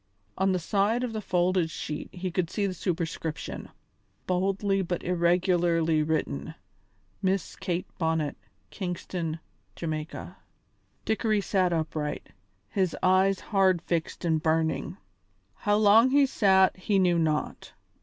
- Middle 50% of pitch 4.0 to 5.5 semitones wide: No, average, 3.1 semitones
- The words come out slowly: Yes, slow, 125 wpm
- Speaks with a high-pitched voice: No, medium, 180 Hz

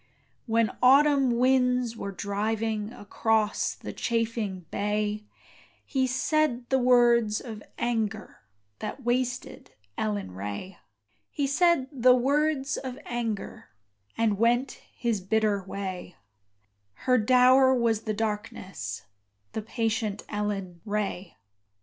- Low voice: No, high, 225 Hz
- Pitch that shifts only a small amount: No, average, 3.4 semitones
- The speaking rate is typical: No, slow, 105 wpm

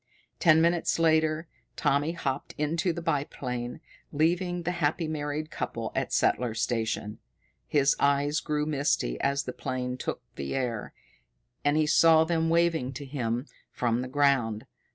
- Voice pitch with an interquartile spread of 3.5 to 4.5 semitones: Yes, average, 4.1 semitones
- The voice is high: No, medium, 145 Hz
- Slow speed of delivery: No, average, 145 wpm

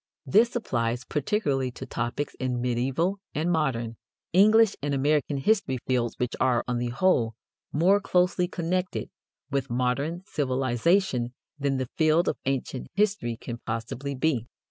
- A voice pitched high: No, low, 135 Hz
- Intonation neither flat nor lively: No, wide, 6.2 semitones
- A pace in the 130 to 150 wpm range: Yes, average, 140 wpm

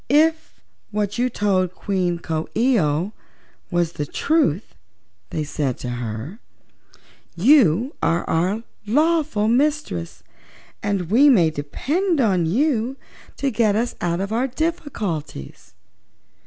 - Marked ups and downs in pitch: Yes, wide, 8.2 semitones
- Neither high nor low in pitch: No, high, 205 Hz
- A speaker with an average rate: No, slow, 120 wpm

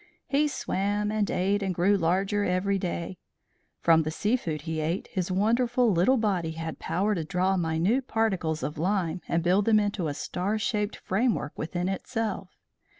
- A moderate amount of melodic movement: Yes, average, 3.7 semitones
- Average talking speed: Yes, average, 170 wpm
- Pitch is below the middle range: No, high, 190 Hz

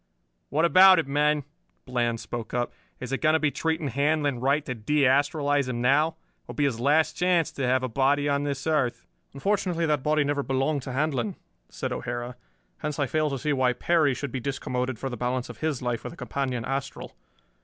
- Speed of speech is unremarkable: No, fast, 210 wpm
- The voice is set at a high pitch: No, medium, 140 Hz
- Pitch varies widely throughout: No, average, 3.1 semitones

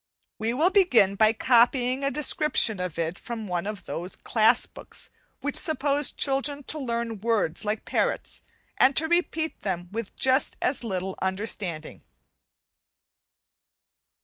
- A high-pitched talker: Yes, high, 230 Hz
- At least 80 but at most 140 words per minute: Yes, slow, 135 wpm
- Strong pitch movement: Yes, wide, 5.9 semitones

